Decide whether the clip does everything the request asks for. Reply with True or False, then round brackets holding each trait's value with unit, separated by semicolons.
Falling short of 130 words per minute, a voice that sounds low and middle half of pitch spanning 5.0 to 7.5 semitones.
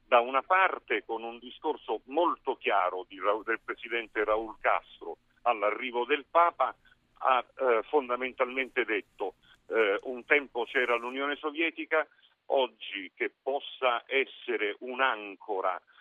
True (115 wpm; 130 Hz; 5.5 semitones)